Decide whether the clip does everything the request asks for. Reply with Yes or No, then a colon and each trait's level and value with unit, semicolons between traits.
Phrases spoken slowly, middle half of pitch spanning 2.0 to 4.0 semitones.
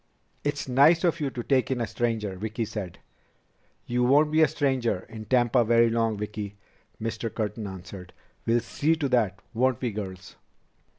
No: average, 170 wpm; average, 3.6 semitones